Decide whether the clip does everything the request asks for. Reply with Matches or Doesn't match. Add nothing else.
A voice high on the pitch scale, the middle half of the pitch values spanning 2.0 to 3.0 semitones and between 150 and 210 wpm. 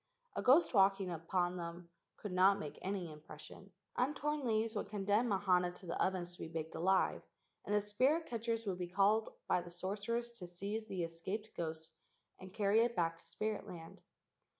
Doesn't match